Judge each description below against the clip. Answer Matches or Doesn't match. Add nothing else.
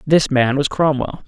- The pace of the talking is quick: Doesn't match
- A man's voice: Matches